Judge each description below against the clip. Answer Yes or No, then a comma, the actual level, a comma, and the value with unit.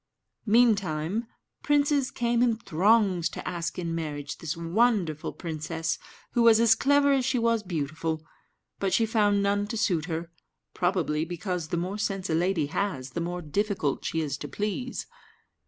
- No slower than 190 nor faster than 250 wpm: No, average, 160 wpm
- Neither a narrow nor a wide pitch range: No, wide, 5.7 semitones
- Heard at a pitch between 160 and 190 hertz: Yes, medium, 185 Hz